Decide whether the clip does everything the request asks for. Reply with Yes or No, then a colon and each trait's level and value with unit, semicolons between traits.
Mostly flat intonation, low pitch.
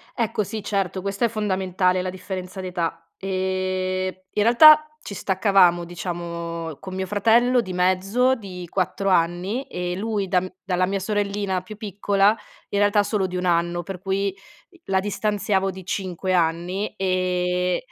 No: narrow, 2.1 semitones; high, 190 Hz